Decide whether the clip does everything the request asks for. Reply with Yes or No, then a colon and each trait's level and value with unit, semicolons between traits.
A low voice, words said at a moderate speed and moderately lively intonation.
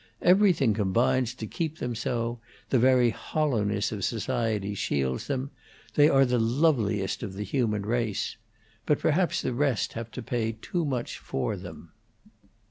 Yes: low, 120 Hz; average, 150 wpm; average, 4.4 semitones